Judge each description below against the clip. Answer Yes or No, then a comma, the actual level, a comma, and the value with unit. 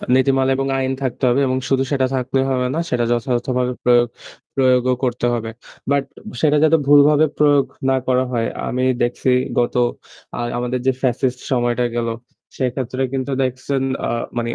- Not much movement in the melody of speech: Yes, narrow, 1.7 semitones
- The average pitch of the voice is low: Yes, low, 130 Hz